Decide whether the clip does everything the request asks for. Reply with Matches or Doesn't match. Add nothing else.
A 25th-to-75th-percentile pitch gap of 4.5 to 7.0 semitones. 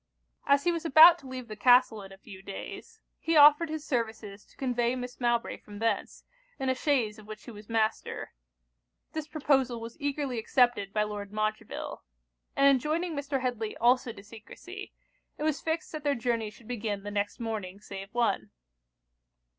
Matches